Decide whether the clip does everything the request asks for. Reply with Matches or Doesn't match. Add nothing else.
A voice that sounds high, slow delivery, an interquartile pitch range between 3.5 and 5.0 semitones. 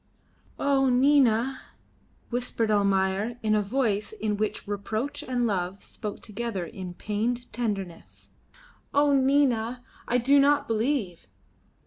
Matches